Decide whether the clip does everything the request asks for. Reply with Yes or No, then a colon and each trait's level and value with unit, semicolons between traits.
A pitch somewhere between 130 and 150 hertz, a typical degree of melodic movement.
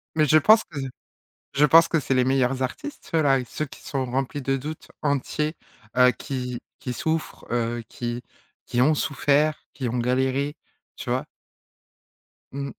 Yes: low, 135 Hz; average, 3.1 semitones